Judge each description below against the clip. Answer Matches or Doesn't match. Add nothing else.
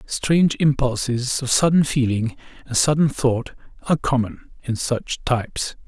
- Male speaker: Matches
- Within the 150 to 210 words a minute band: Doesn't match